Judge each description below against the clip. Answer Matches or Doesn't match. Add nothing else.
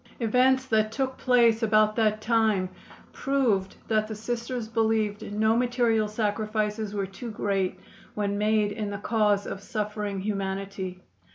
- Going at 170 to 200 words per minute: Doesn't match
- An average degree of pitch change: Doesn't match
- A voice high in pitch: Matches